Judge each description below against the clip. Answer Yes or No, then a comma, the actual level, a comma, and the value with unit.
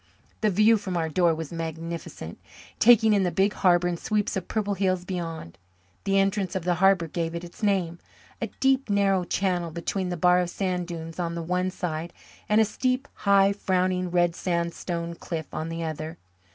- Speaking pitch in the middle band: Yes, medium, 180 Hz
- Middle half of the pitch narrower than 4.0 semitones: Yes, narrow, 2.6 semitones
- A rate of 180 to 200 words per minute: Yes, average, 190 wpm